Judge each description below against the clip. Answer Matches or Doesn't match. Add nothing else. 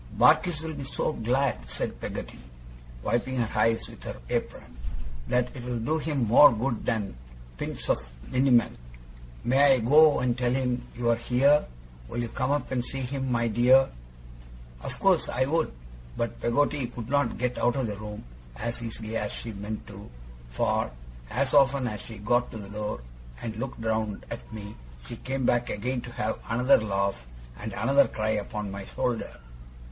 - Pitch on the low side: Matches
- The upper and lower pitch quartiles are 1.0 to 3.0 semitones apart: Doesn't match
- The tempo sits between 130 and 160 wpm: Doesn't match